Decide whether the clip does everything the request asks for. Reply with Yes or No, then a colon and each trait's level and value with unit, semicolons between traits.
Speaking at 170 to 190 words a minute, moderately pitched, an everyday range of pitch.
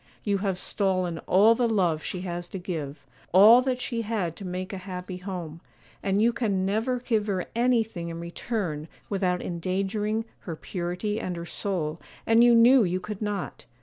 No: average, 180 wpm; high, 195 Hz; average, 3.8 semitones